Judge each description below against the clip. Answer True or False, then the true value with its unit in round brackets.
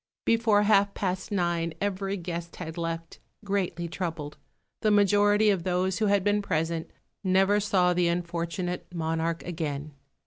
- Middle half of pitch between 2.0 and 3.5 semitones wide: True (3.2 semitones)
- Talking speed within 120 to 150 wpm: True (140 wpm)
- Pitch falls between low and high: True (180 Hz)